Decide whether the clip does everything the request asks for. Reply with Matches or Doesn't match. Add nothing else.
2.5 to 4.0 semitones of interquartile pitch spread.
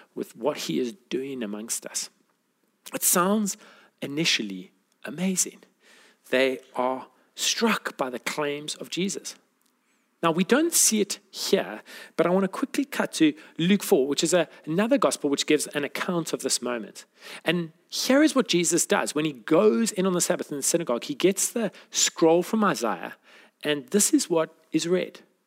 Doesn't match